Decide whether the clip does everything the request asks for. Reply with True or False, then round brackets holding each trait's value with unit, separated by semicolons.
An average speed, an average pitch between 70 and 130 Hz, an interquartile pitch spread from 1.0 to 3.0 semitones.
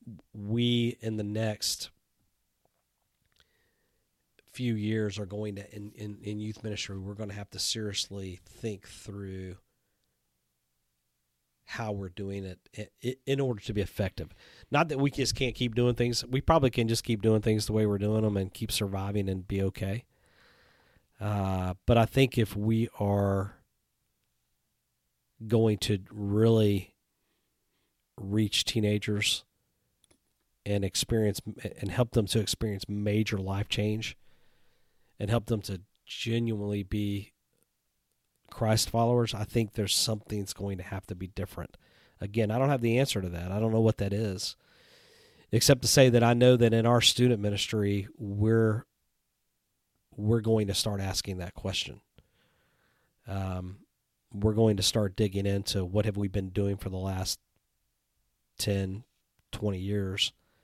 True (145 wpm; 105 Hz; 2.5 semitones)